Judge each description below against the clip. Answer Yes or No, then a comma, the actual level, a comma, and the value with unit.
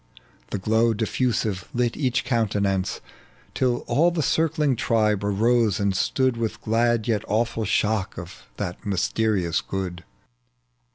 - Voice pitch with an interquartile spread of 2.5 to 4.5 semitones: Yes, average, 3.2 semitones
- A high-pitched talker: No, low, 110 Hz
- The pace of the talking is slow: Yes, slow, 125 wpm